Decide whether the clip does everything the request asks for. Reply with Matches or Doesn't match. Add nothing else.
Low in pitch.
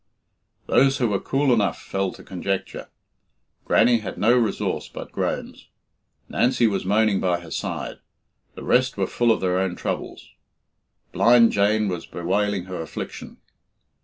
Matches